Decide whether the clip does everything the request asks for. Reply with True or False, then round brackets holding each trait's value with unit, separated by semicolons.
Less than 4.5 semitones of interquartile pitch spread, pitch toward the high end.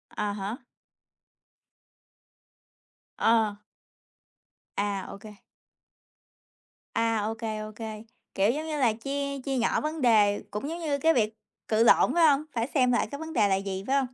False (4.8 semitones; 230 Hz)